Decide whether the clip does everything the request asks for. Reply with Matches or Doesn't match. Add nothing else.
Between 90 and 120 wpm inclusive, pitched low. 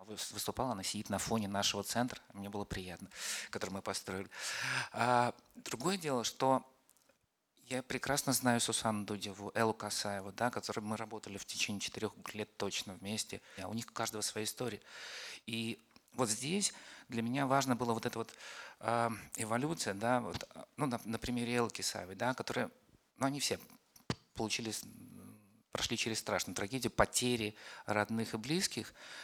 Doesn't match